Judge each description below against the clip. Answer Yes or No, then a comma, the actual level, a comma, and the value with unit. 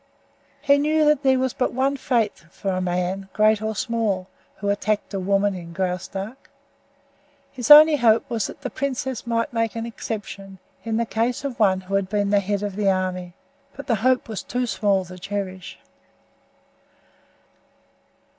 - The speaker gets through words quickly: No, average, 170 wpm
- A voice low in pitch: No, high, 210 Hz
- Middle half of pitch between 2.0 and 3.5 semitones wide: No, average, 4.0 semitones